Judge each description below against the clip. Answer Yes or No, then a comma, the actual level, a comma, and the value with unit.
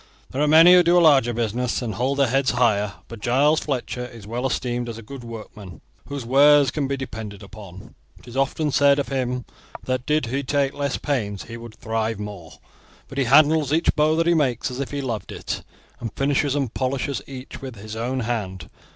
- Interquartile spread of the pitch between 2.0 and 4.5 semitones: Yes, average, 3.6 semitones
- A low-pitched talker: Yes, low, 130 Hz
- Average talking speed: No, fast, 210 wpm